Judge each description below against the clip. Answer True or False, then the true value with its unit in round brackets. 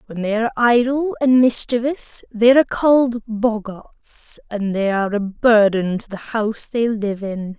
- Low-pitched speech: False (225 Hz)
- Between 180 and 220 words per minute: False (165 wpm)